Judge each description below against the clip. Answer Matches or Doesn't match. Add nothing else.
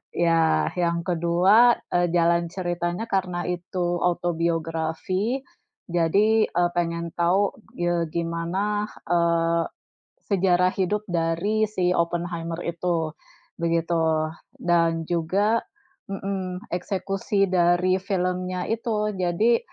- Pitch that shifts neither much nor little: Doesn't match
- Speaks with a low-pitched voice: Doesn't match